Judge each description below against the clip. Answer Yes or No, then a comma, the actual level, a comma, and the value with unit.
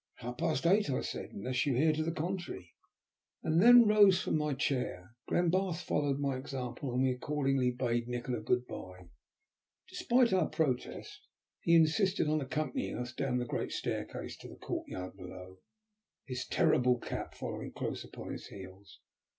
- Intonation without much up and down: No, average, 4.8 semitones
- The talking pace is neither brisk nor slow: Yes, average, 165 wpm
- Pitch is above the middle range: No, low, 135 Hz